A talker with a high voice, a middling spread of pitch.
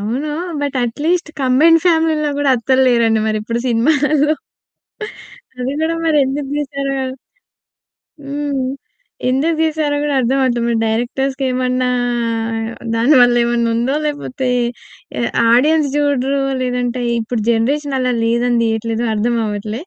Yes: very high, 260 Hz; average, 3.6 semitones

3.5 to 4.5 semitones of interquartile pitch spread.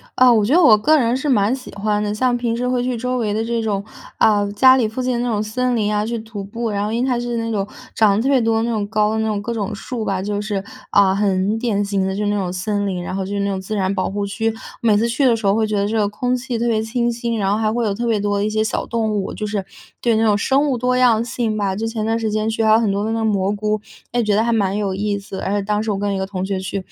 No: narrow, 2.4 semitones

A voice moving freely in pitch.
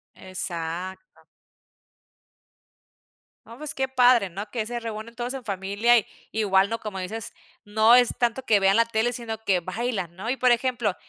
No: average, 3.6 semitones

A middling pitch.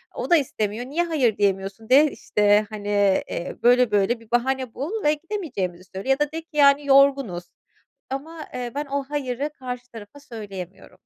No: very high, 250 Hz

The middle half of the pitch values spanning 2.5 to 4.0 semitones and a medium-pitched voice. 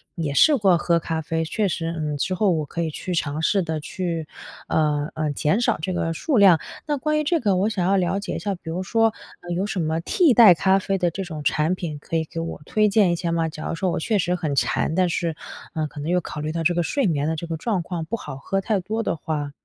Yes: average, 3.5 semitones; medium, 170 Hz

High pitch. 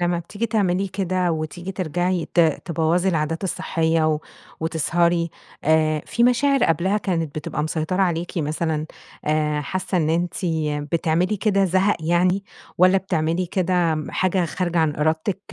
No: medium, 170 Hz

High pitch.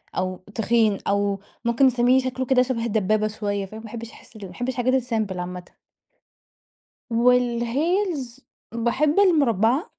Yes: high, 235 Hz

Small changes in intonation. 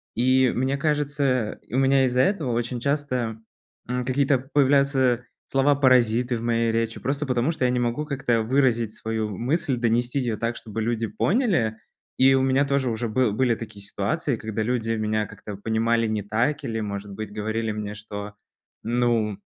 No: average, 3.2 semitones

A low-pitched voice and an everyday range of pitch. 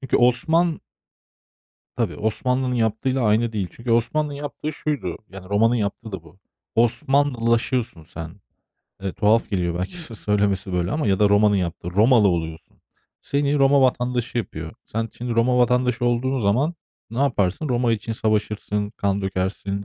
Yes: low, 115 Hz; average, 4.0 semitones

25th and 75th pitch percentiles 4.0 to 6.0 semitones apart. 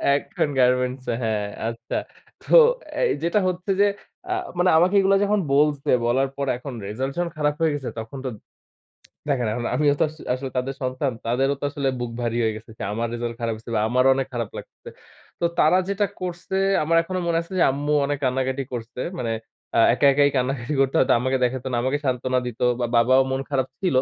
No: average, 3.4 semitones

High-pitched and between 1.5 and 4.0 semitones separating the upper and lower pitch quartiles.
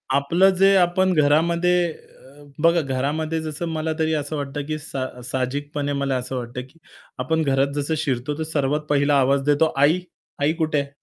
No: medium, 145 Hz; narrow, 2.5 semitones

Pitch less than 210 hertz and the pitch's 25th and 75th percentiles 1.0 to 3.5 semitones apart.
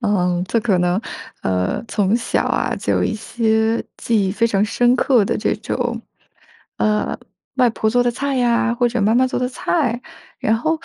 No: high, 230 Hz; average, 2.8 semitones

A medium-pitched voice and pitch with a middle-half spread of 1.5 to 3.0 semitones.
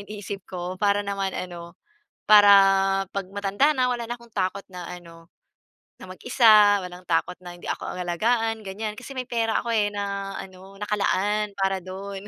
No: high, 200 Hz; narrow, 2.4 semitones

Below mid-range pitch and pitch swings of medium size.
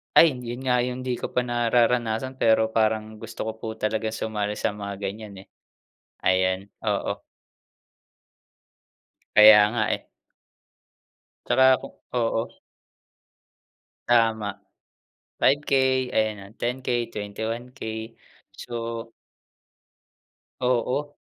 No: low, 115 Hz; narrow, 2.3 semitones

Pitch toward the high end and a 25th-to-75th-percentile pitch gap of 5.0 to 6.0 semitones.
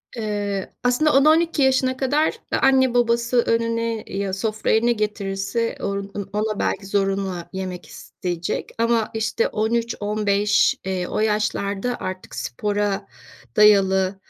No: high, 210 Hz; average, 3.1 semitones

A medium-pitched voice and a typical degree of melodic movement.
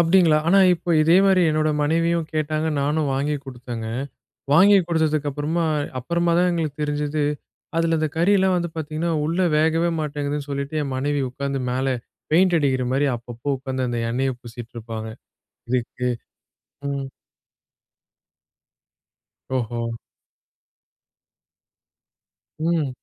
Yes: medium, 150 Hz; average, 3.8 semitones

